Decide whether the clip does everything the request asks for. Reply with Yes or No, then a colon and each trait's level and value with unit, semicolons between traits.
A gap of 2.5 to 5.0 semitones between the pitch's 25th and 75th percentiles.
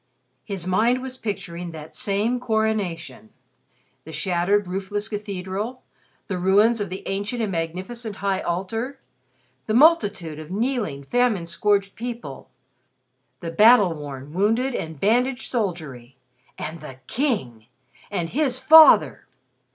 No: wide, 5.6 semitones